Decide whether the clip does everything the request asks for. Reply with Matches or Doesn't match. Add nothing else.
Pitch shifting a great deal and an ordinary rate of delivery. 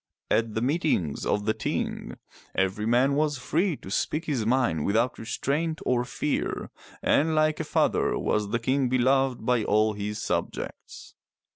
Doesn't match